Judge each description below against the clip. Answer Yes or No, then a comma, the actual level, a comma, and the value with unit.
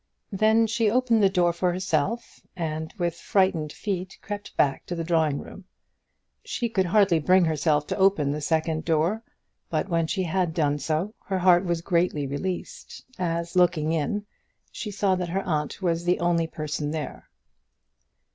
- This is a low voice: No, medium, 175 Hz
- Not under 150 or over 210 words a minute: Yes, average, 165 wpm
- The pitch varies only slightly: No, average, 3.3 semitones